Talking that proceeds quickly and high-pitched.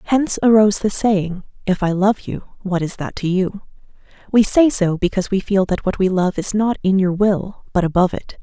Yes: fast, 220 wpm; high, 195 Hz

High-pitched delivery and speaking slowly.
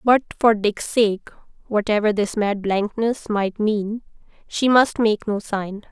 Yes: high, 215 Hz; slow, 130 wpm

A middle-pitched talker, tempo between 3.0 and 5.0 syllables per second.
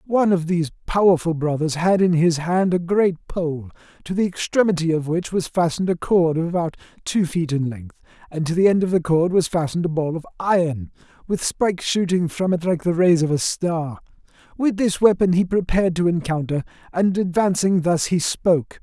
No: medium, 170 Hz; 5.3 syllables/s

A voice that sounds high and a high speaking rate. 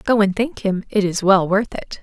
Yes: high, 200 Hz; fast, 265 wpm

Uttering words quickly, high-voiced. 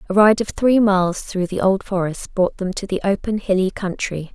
Yes: fast, 220 wpm; high, 195 Hz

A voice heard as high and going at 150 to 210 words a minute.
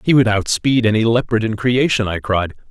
No: low, 110 Hz; average, 200 wpm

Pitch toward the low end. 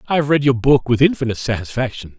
Yes: low, 125 Hz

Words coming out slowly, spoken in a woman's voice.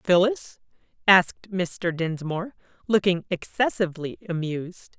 Yes: slow, 85 wpm; female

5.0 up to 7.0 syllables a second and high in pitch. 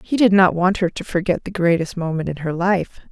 No: 5.5 syllables/s; medium, 180 Hz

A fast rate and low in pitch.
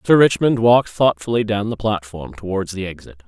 No: average, 185 wpm; low, 105 Hz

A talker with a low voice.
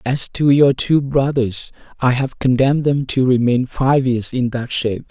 Yes: low, 130 Hz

